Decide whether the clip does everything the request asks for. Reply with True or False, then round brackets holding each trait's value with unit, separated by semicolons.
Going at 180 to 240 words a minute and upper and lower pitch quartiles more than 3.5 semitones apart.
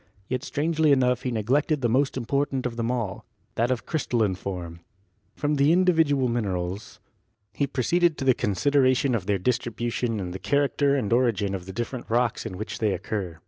True (185 wpm; 5.2 semitones)